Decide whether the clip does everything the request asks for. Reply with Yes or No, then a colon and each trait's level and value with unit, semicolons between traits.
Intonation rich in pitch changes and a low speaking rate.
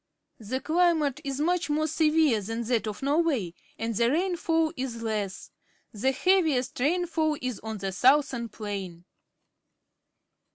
Yes: wide, 5.9 semitones; slow, 130 wpm